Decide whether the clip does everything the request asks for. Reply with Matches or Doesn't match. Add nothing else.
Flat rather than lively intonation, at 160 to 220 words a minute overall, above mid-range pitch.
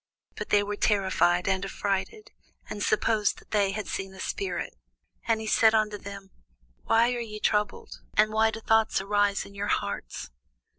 Matches